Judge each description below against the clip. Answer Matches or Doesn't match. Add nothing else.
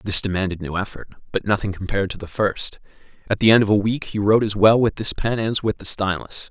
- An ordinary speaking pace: Doesn't match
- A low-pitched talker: Matches